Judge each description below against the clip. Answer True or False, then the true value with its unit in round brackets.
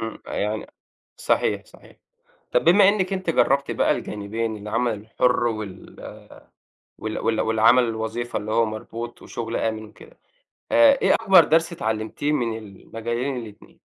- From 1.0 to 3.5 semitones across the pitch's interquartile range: False (4.3 semitones)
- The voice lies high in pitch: False (115 Hz)